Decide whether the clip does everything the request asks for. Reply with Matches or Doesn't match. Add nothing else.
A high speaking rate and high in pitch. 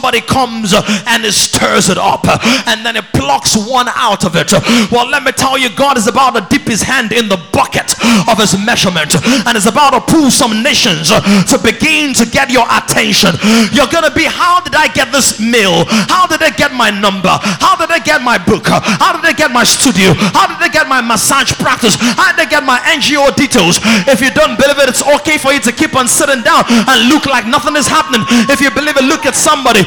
Matches